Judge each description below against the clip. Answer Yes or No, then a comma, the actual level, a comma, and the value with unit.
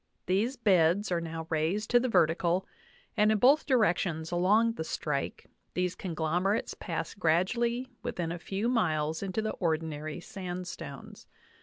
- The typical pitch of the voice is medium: Yes, medium, 180 Hz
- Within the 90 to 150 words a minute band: Yes, average, 140 wpm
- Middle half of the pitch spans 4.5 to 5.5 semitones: Yes, average, 4.8 semitones